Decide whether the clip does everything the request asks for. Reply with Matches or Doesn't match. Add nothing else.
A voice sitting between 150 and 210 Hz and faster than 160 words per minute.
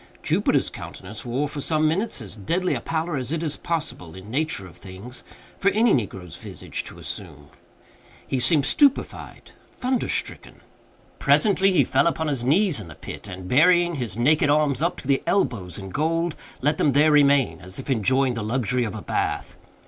Doesn't match